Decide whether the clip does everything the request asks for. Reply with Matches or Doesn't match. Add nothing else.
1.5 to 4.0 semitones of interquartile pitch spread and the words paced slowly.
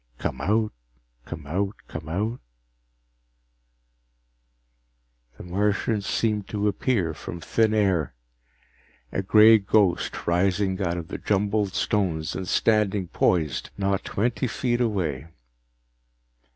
Matches